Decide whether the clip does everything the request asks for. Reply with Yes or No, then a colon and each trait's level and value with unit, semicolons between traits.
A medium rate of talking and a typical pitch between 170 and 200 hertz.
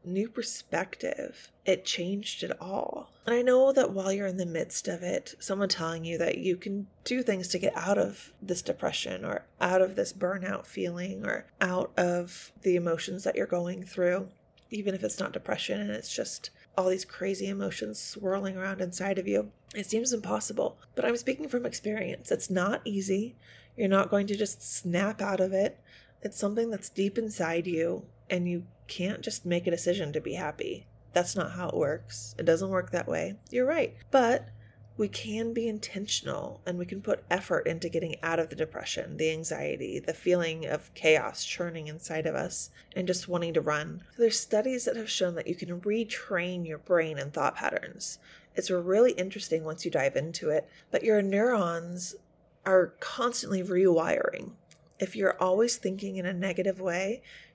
Yes: average, 185 wpm; medium, 185 Hz